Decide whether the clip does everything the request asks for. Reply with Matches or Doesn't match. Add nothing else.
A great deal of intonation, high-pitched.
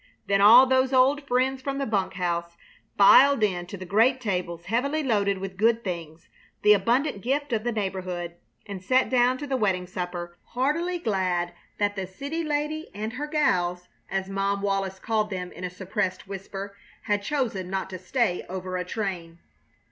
Matches